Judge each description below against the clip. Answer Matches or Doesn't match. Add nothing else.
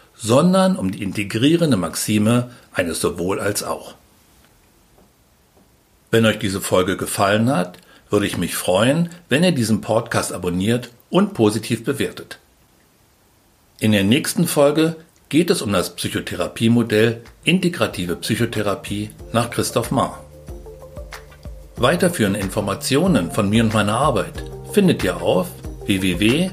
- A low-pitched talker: Matches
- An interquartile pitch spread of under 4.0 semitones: Doesn't match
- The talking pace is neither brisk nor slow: Doesn't match